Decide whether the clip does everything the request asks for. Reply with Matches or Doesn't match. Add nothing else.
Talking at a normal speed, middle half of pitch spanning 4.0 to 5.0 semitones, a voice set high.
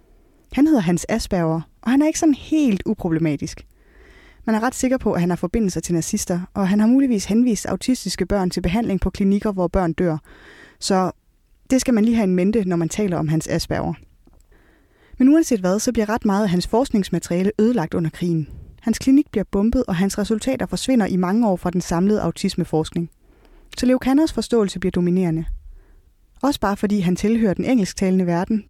Matches